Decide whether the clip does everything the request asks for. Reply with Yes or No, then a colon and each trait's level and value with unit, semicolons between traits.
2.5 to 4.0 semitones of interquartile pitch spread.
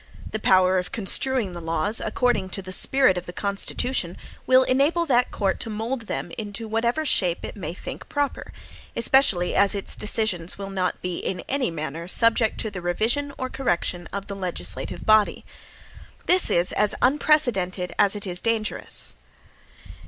No: average, 5.2 semitones